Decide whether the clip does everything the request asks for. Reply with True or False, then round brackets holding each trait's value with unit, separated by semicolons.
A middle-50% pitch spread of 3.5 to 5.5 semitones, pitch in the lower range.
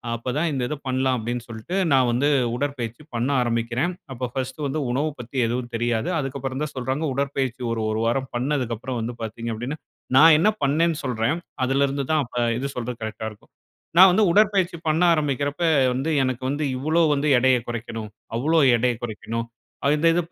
True (3.8 semitones; 130 Hz)